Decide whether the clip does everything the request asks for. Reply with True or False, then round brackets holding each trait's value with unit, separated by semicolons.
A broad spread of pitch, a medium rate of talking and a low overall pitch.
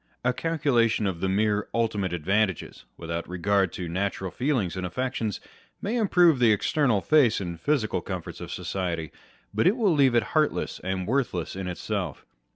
True (6.0 semitones; 160 wpm; 105 Hz)